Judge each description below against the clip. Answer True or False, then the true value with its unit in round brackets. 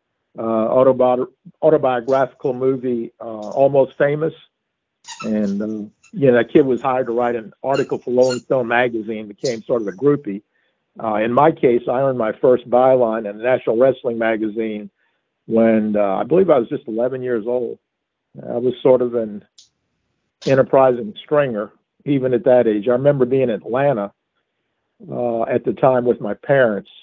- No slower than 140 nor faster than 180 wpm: True (165 wpm)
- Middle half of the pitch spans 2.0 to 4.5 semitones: True (2.9 semitones)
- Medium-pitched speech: False (125 Hz)